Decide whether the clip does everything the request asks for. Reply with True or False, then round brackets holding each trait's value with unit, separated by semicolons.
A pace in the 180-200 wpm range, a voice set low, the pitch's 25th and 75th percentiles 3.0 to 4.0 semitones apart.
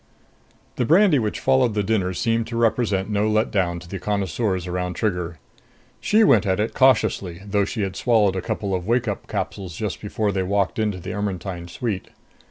True (190 wpm; 100 Hz; 3.3 semitones)